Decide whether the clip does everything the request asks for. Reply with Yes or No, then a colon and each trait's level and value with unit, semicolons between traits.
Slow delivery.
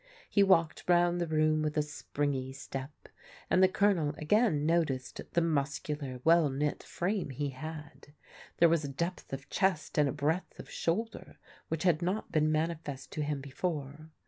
No: average, 170 wpm